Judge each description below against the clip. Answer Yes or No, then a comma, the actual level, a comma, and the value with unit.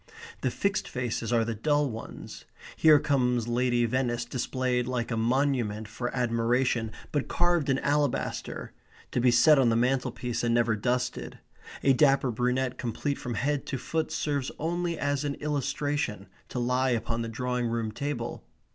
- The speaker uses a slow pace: No, average, 160 wpm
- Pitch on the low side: Yes, low, 125 Hz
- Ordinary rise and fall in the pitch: Yes, average, 3.2 semitones